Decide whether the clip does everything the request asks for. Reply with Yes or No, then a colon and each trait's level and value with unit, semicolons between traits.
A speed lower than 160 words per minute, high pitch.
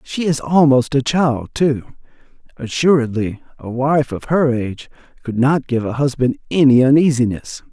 No: average, 150 wpm; low, 135 Hz